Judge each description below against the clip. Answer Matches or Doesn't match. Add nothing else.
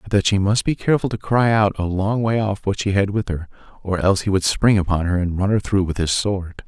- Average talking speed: Doesn't match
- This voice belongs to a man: Matches